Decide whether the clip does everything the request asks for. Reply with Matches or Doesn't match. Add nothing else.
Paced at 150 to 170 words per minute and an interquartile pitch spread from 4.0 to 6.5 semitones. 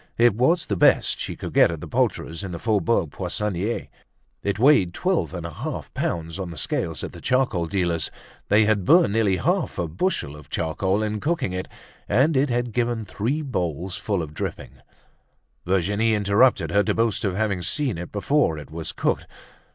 Doesn't match